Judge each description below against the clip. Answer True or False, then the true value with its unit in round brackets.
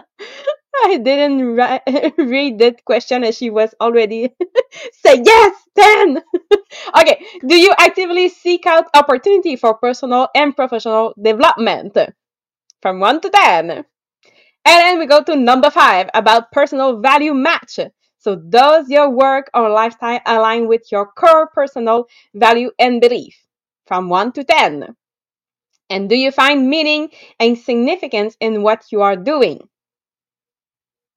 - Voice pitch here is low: False (270 Hz)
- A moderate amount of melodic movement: False (6.1 semitones)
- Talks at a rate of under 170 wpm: True (135 wpm)